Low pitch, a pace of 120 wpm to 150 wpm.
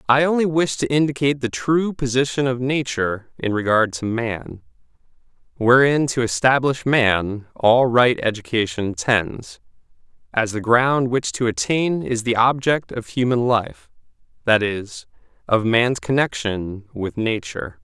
Yes: low, 120 Hz; average, 140 wpm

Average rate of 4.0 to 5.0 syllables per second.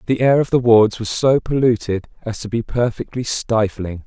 Yes: 4.8 syllables/s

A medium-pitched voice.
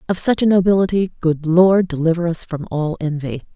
Yes: medium, 170 Hz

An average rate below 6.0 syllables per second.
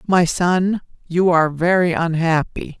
Yes: 4.2 syllables/s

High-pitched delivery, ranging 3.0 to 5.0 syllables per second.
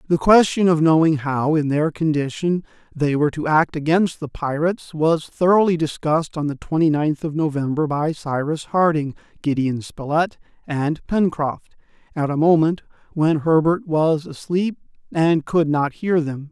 No: medium, 155 Hz; 4.6 syllables/s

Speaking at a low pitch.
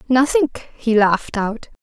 No: high, 240 Hz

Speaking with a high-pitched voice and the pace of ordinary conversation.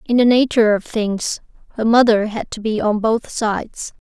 Yes: high, 220 Hz; average, 190 wpm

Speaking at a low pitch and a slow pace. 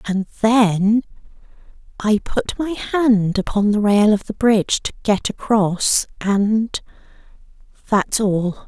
No: high, 210 Hz; slow, 120 wpm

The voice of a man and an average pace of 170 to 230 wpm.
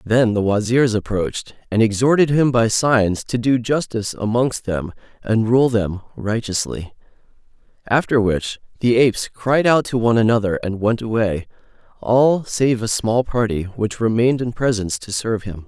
No: male; average, 160 wpm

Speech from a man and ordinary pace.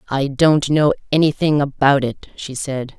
No: female; average, 160 wpm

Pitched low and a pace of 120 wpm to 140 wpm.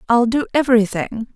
No: high, 235 Hz; slow, 135 wpm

